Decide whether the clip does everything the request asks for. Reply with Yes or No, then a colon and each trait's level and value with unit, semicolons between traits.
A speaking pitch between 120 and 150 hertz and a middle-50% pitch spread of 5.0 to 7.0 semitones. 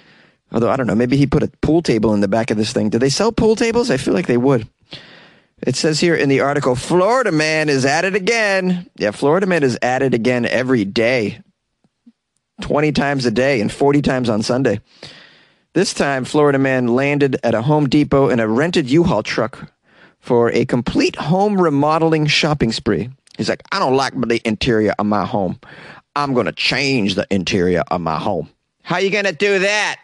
Yes: medium, 140 Hz; wide, 5.4 semitones